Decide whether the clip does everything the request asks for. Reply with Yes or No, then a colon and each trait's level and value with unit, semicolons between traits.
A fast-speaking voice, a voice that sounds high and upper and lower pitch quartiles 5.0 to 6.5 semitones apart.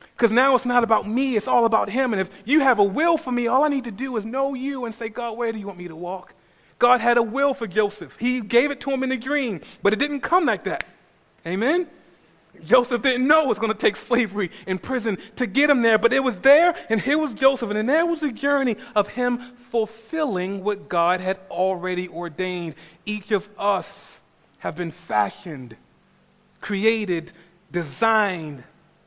Yes: fast, 210 wpm; high, 225 Hz; wide, 5.5 semitones